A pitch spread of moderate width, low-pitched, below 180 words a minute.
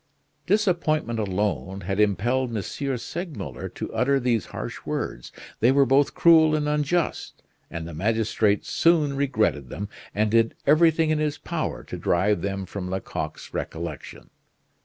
No: wide, 7.0 semitones; low, 120 Hz; average, 140 wpm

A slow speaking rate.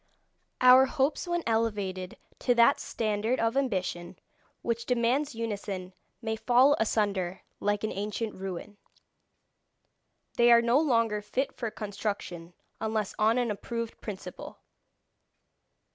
Yes: slow, 115 wpm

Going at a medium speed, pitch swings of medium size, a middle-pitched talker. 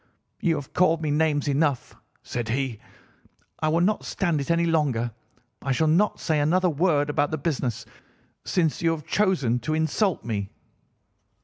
Yes: average, 165 wpm; average, 3.5 semitones; medium, 155 Hz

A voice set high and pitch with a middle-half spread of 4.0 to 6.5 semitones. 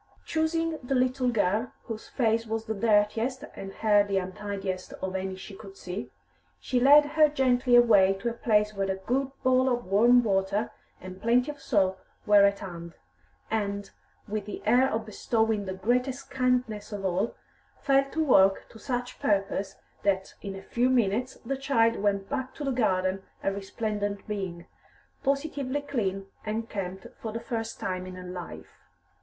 Yes: high, 215 Hz; average, 4.3 semitones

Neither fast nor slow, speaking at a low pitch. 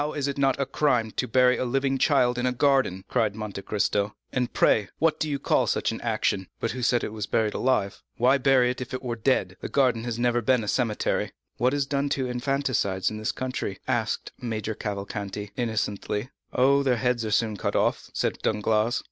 No: fast, 215 wpm; low, 120 Hz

